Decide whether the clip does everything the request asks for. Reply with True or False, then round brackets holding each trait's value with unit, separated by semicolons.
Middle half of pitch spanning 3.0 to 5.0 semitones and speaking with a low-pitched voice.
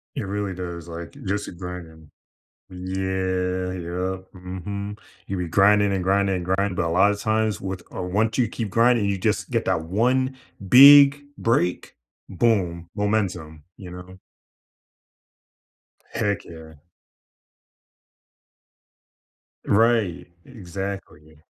False (2.5 semitones; 95 Hz)